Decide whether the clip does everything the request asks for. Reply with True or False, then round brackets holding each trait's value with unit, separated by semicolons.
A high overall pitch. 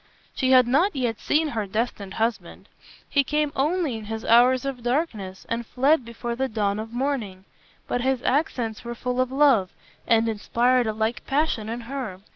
True (240 Hz)